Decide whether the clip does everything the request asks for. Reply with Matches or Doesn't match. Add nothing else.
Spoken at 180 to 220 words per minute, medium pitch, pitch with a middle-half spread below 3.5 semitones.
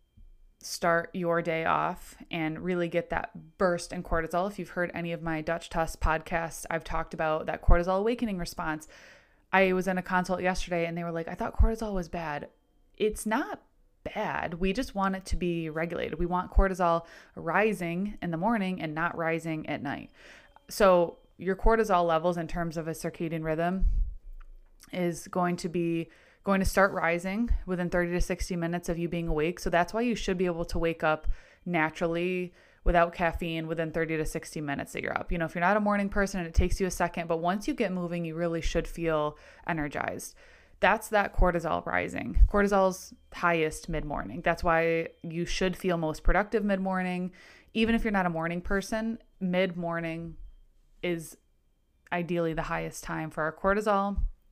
Matches